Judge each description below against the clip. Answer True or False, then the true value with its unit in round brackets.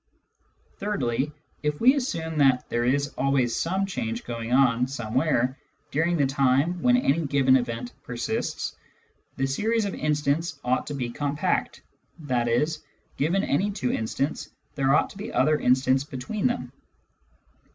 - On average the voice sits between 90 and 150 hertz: True (140 Hz)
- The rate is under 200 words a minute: True (140 wpm)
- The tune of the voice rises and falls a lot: False (4.5 semitones)